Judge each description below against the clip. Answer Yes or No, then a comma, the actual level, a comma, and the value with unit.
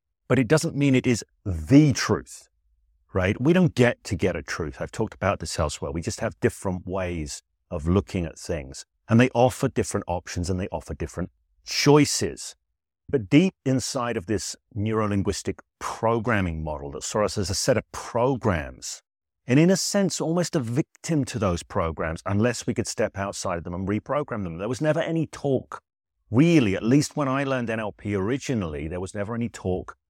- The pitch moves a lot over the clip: Yes, wide, 6.6 semitones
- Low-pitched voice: Yes, low, 110 Hz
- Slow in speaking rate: No, average, 190 wpm